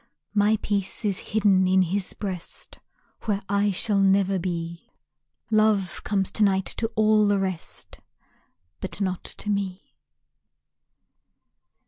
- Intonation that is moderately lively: No, narrow, 1.8 semitones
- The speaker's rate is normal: No, slow, 120 wpm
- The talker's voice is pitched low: No, high, 195 Hz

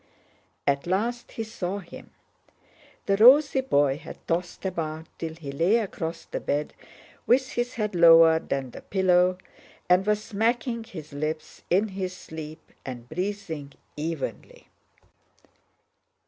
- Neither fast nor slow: No, slow, 130 wpm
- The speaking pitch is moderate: Yes, medium, 180 Hz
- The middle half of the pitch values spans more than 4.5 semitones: Yes, average, 5.1 semitones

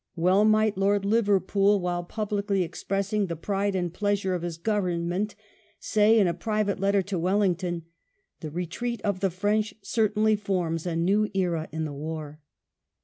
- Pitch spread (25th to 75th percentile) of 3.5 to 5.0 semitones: No, average, 3.1 semitones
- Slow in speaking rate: No, average, 155 wpm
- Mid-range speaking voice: No, high, 195 Hz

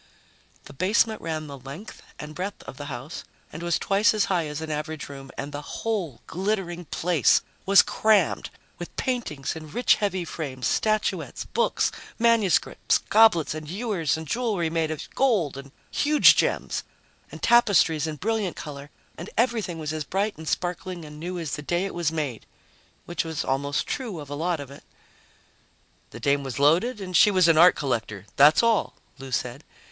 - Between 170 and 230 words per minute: Yes, average, 180 wpm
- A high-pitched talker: No, medium, 165 Hz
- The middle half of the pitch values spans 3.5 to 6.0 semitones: Yes, wide, 5.4 semitones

